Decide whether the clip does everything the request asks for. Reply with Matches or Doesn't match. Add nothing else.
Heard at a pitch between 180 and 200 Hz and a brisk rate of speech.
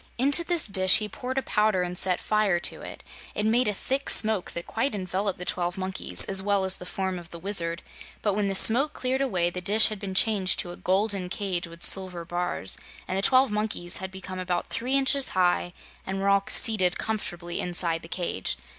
Matches